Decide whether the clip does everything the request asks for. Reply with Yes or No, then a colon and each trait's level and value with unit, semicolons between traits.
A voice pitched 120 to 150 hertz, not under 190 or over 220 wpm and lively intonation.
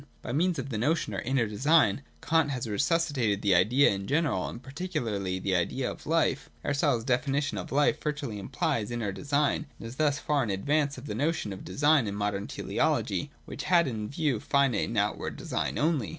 Yes: low, 135 Hz; average, 200 wpm; wide, 5.9 semitones